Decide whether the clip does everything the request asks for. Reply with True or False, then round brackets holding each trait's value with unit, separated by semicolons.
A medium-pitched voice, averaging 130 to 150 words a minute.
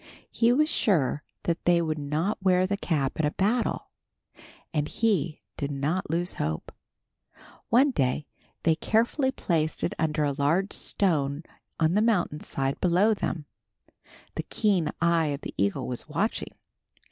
True (165 Hz; 145 wpm)